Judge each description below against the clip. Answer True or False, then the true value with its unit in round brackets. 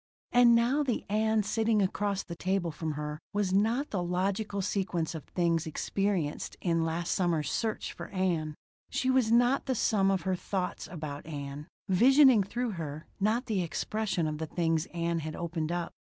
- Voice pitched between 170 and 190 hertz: True (185 Hz)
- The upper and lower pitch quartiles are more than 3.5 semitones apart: True (5.0 semitones)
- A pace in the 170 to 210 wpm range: True (175 wpm)